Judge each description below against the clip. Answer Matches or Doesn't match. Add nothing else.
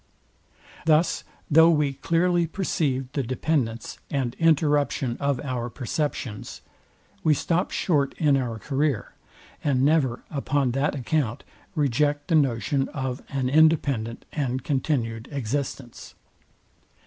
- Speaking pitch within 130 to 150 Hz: Matches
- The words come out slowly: Matches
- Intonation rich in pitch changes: Doesn't match